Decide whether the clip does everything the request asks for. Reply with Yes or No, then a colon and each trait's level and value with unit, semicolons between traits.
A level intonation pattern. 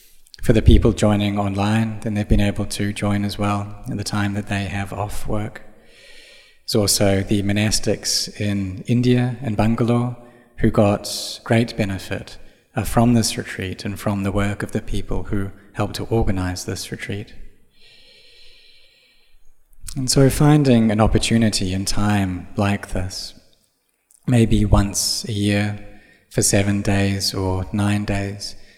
Yes: narrow, 2.2 semitones